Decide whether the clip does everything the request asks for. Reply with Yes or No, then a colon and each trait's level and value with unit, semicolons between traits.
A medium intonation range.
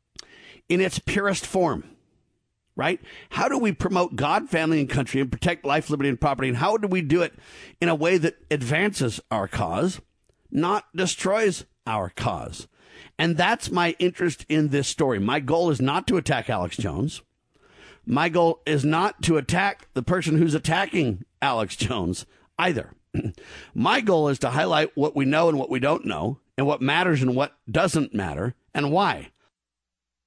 Yes: average, 4.4 semitones